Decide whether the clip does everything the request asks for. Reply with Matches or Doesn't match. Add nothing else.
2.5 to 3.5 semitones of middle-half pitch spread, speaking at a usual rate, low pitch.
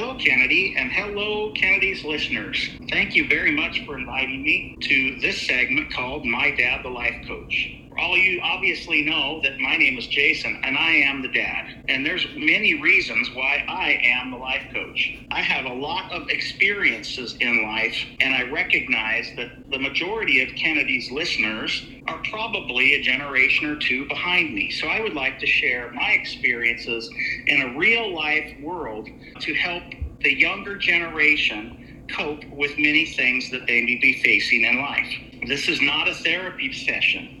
Matches